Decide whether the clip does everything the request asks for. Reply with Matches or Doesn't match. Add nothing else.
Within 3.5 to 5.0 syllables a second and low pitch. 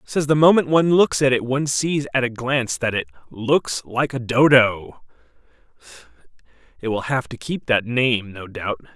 Matches